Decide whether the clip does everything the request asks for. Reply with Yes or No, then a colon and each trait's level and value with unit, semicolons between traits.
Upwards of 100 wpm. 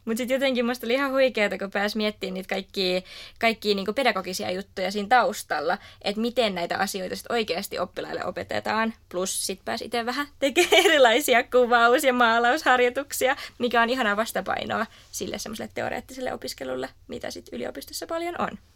Yes: fast, 155 wpm